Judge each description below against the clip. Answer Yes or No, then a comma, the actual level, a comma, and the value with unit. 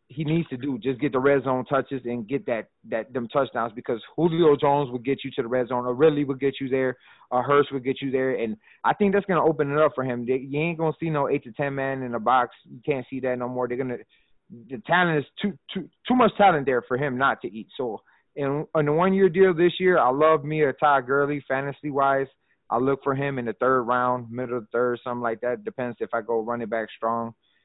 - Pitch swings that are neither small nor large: Yes, average, 3.3 semitones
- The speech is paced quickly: Yes, fast, 260 wpm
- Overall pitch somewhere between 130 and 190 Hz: Yes, low, 135 Hz